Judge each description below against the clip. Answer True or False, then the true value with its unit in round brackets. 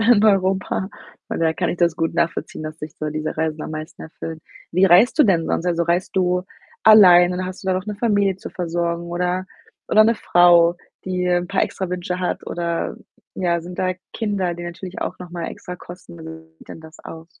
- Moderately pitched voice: True (175 Hz)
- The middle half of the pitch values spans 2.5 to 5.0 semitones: False (1.9 semitones)